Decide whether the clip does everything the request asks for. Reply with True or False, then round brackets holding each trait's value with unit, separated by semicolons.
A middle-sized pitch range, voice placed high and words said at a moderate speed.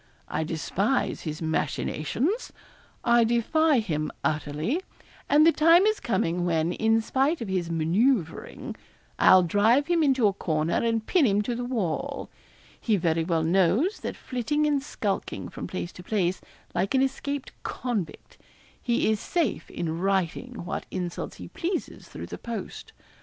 False (7.8 semitones; 220 Hz; 150 wpm)